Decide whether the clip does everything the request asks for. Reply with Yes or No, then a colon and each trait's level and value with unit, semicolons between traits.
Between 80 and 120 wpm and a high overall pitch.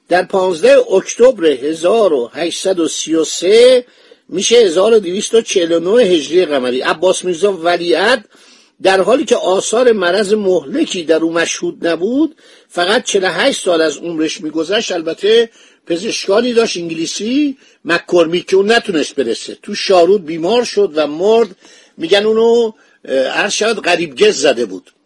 Yes: average, 115 wpm; high, 205 Hz